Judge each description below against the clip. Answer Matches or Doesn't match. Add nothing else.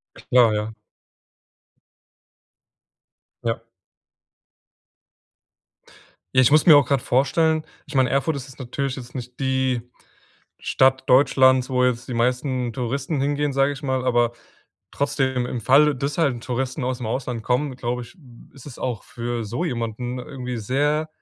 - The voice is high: Doesn't match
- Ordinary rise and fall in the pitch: Doesn't match